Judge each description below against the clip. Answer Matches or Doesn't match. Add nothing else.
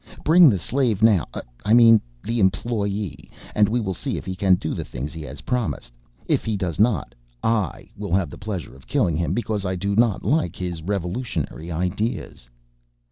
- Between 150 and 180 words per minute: Doesn't match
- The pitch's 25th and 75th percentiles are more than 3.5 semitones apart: Matches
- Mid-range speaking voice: Doesn't match